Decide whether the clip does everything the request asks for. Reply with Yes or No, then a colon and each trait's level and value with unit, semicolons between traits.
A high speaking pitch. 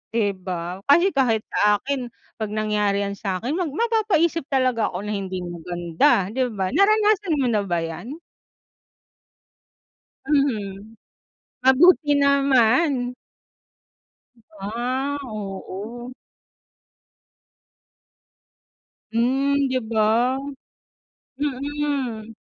Yes: high, 245 Hz